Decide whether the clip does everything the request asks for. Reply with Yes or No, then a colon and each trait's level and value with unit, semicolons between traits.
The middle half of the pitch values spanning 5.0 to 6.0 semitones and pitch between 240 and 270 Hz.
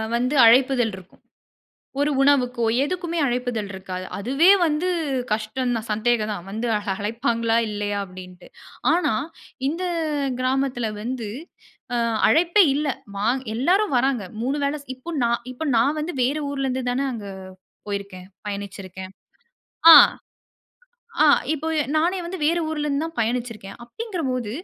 Yes: wide, 5.4 semitones; high, 245 Hz